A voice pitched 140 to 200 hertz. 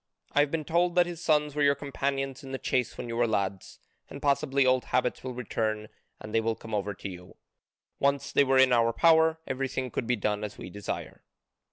No: low, 130 Hz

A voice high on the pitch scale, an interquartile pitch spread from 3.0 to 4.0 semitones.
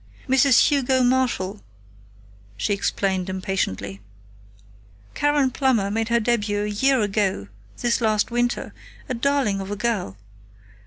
No: high, 220 Hz; average, 4.5 semitones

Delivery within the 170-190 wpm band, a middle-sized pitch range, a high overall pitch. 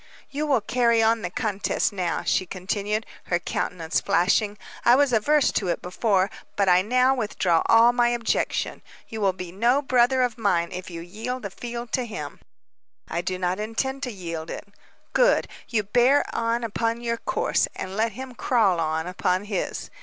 Yes: average, 180 wpm; average, 4.5 semitones; high, 215 Hz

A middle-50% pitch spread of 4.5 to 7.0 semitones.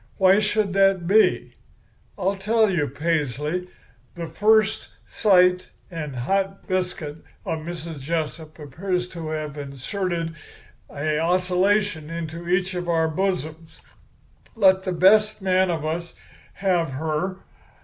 No: average, 3.3 semitones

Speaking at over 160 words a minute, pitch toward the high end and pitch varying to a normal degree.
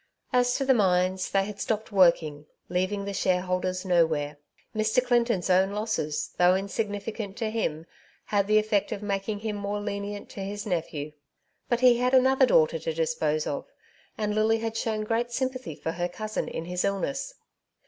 Yes: average, 170 wpm; high, 205 Hz; average, 3.7 semitones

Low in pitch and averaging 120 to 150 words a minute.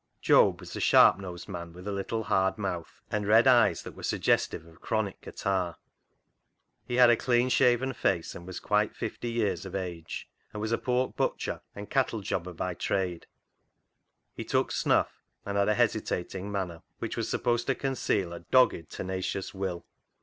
No: low, 100 Hz; average, 175 wpm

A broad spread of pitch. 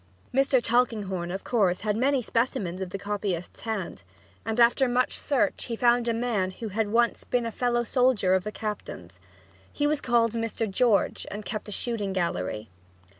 No: average, 3.8 semitones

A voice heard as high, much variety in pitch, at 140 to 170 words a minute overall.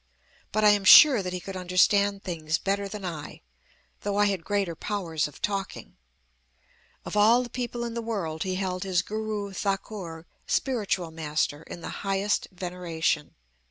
No: high, 195 Hz; average, 3.2 semitones; average, 160 wpm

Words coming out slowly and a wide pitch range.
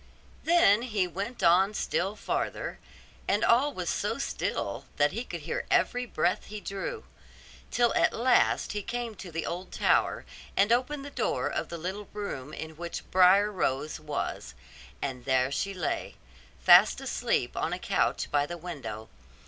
No: average, 165 wpm; wide, 6.5 semitones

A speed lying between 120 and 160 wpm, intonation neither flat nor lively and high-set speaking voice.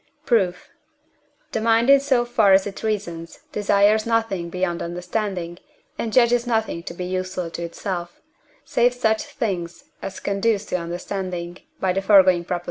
Yes: average, 150 wpm; average, 4.0 semitones; high, 195 Hz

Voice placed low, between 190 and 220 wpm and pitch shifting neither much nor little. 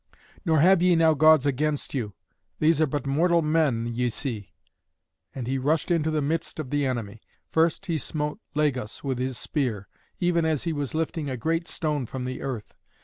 No: medium, 150 Hz; average, 195 wpm; average, 3.8 semitones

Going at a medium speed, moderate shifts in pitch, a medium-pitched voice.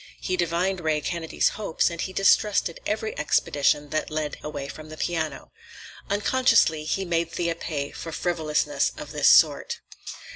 Yes: average, 150 wpm; average, 3.5 semitones; medium, 170 Hz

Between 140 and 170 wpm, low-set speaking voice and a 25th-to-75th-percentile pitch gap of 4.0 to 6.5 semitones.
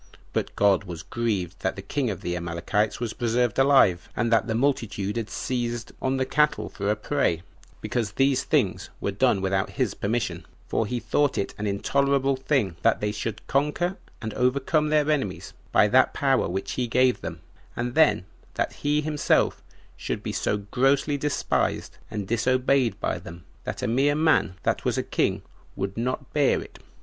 No: average, 180 wpm; low, 120 Hz; wide, 5.4 semitones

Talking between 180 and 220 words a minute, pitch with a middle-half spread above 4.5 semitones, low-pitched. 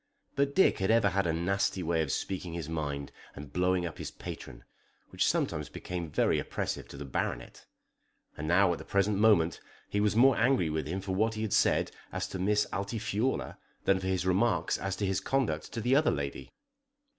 No: fast, 205 wpm; average, 4.1 semitones; very low, 95 Hz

